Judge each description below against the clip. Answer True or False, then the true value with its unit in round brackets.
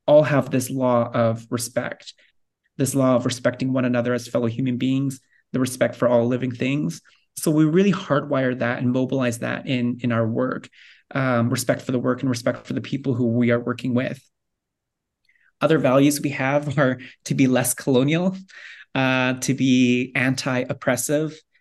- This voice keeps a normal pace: True (175 wpm)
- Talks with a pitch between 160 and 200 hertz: False (130 Hz)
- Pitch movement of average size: False (1.8 semitones)